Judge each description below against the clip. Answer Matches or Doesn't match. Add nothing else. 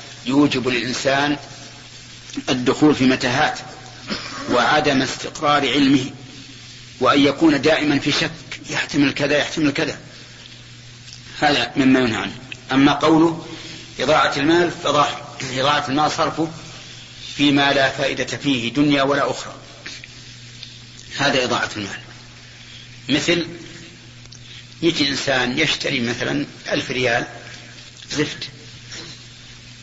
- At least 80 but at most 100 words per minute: Matches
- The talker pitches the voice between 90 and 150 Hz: Matches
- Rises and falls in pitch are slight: Doesn't match